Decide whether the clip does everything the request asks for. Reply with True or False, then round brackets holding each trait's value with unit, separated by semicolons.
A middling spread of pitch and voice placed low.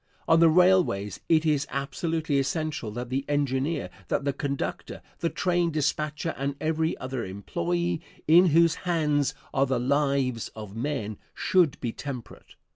False (3.8 semitones; 145 Hz)